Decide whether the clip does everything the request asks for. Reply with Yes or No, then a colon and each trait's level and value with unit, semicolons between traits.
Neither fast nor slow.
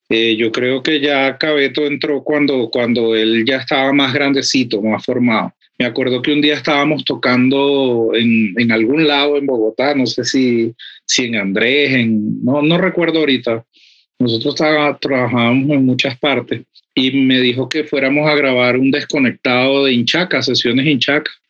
Yes: average, 165 wpm